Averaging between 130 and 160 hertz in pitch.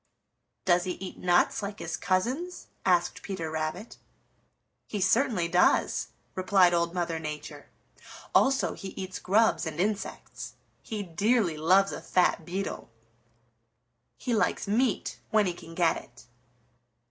No: medium, 185 Hz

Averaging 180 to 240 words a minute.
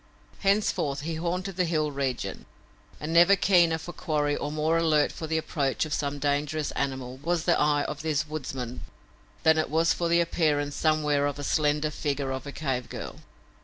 Yes: average, 185 wpm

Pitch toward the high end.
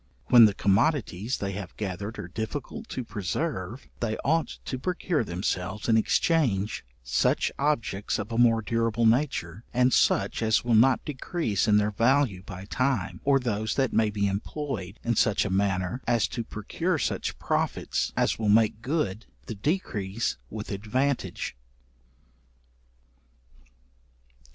No: low, 110 Hz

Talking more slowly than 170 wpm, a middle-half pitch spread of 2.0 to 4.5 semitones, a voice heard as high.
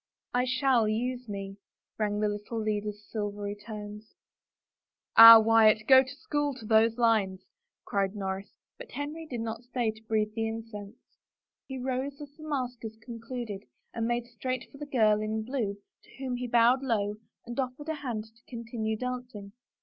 No: average, 175 wpm; average, 3.0 semitones; high, 225 Hz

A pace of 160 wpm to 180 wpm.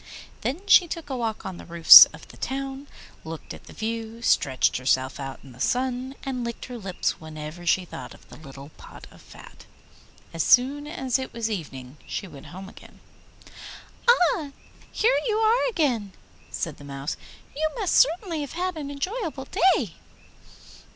Yes: average, 170 wpm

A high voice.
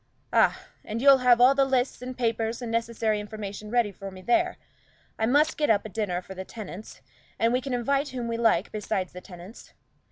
Yes: high, 230 Hz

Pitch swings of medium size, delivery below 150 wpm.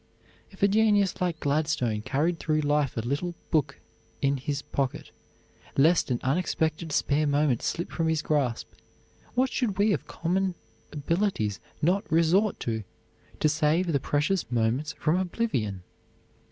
Yes: average, 4.3 semitones; average, 140 wpm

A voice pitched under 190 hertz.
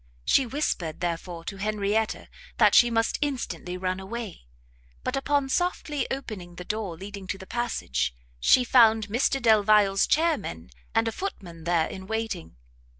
No: high, 210 Hz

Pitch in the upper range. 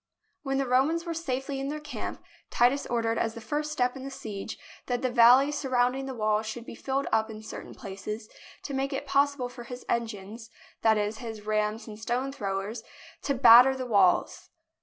Yes: high, 245 Hz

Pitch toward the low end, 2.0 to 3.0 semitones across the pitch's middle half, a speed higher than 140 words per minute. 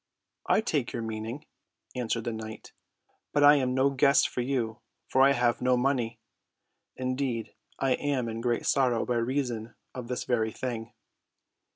Yes: low, 125 Hz; narrow, 2.6 semitones; average, 160 wpm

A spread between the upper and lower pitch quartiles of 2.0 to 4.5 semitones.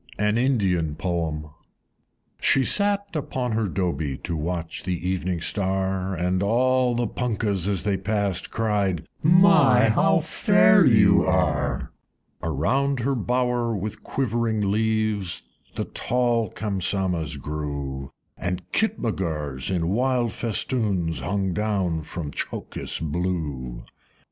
No: wide, 5.5 semitones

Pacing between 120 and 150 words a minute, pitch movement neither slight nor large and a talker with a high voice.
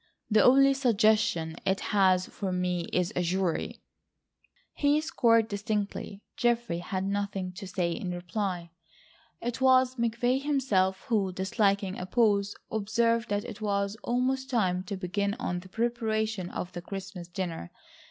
Yes: average, 140 wpm; average, 4.0 semitones; high, 200 Hz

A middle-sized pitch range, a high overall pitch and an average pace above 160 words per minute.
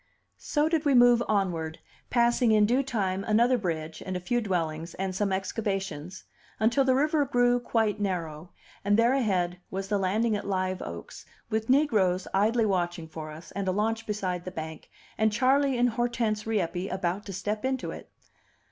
Yes: average, 4.6 semitones; high, 205 Hz; average, 175 wpm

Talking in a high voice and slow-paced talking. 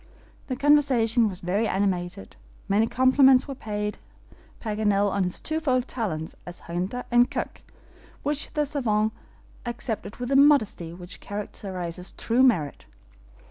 Yes: high, 220 Hz; slow, 130 wpm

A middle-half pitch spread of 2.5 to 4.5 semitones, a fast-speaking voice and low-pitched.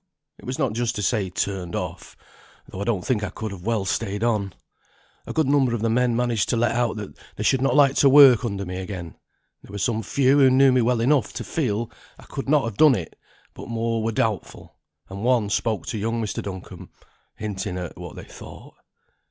Yes: average, 4.0 semitones; fast, 220 wpm; low, 115 Hz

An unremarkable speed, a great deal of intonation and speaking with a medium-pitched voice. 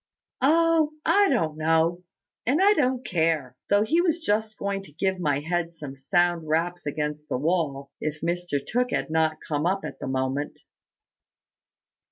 Yes: average, 165 wpm; wide, 6.1 semitones; medium, 170 Hz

